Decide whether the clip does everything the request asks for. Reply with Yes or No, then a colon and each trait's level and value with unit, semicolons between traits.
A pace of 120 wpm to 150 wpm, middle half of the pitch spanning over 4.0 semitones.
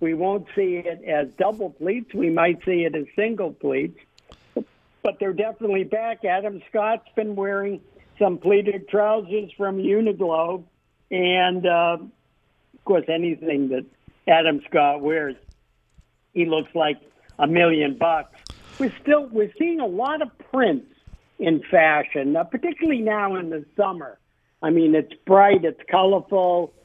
Yes: average, 145 wpm; average, 4.6 semitones